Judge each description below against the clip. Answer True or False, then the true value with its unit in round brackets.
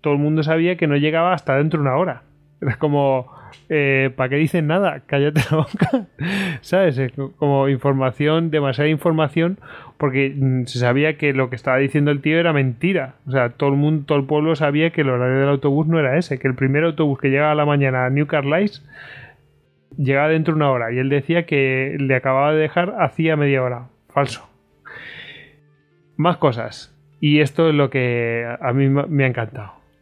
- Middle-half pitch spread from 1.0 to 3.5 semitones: True (2.7 semitones)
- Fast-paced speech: True (195 wpm)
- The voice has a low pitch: False (145 Hz)